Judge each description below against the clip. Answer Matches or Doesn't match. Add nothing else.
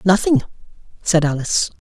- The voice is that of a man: Matches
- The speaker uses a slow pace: Matches